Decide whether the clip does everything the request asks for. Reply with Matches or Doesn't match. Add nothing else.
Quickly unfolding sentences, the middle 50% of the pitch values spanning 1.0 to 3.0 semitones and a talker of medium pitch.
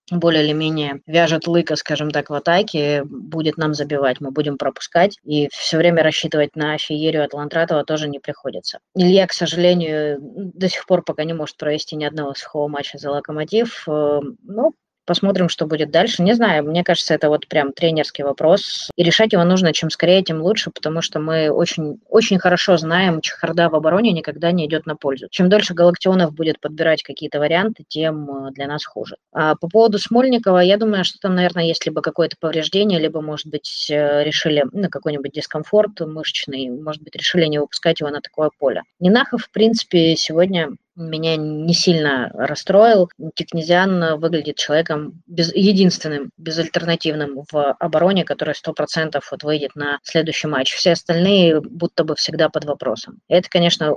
Matches